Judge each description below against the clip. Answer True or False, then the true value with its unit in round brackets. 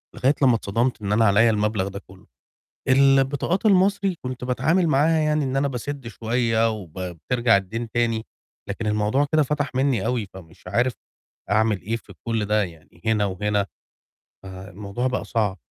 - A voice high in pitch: False (115 Hz)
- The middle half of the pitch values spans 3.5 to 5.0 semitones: True (4.6 semitones)